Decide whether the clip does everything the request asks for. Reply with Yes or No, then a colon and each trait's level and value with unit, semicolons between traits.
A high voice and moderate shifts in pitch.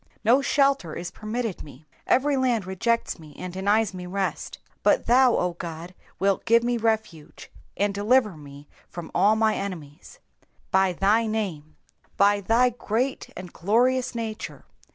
Yes: high, 205 Hz; average, 4.6 semitones